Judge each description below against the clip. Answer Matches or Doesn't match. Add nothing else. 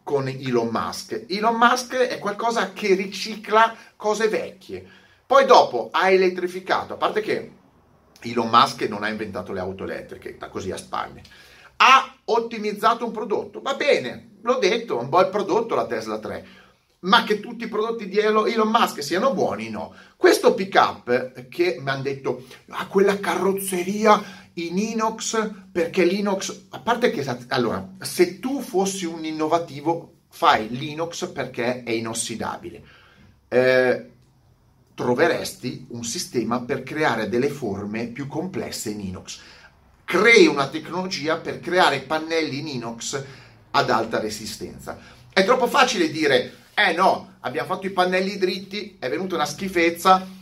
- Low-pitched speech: Doesn't match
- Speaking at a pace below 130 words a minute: Doesn't match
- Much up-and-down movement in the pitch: Matches